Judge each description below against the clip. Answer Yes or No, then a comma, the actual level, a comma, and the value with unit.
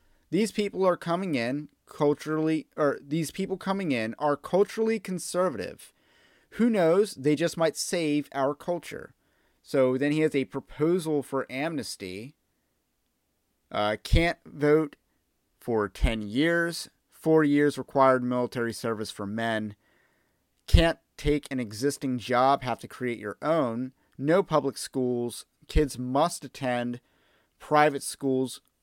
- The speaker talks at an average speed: No, slow, 125 wpm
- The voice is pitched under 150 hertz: Yes, medium, 140 Hz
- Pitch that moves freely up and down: No, average, 4.8 semitones